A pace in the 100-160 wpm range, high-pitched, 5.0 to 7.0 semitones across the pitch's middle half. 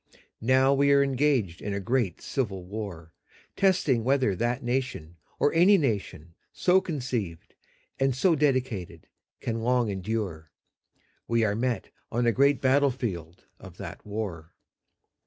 No: slow, 135 wpm; low, 120 Hz; wide, 5.4 semitones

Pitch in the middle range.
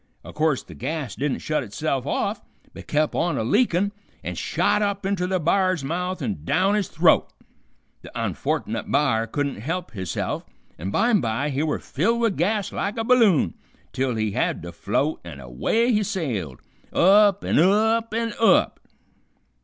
Yes: medium, 165 Hz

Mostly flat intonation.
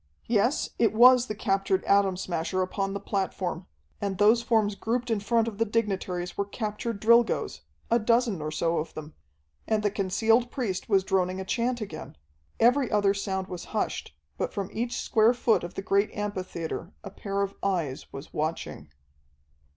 No: average, 3.4 semitones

